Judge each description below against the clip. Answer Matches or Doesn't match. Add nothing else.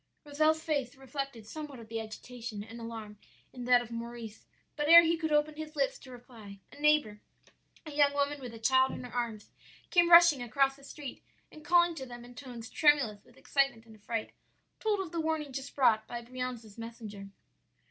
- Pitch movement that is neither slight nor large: Matches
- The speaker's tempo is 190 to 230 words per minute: Matches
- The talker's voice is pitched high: Matches